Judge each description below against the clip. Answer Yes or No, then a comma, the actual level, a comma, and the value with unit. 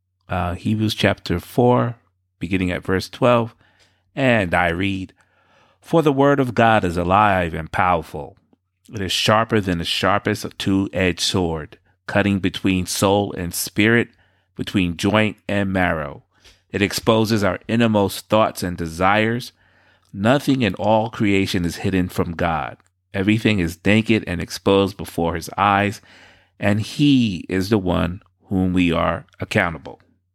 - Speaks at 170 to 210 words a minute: No, average, 140 wpm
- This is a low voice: Yes, very low, 95 Hz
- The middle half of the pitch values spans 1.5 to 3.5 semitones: Yes, average, 3.1 semitones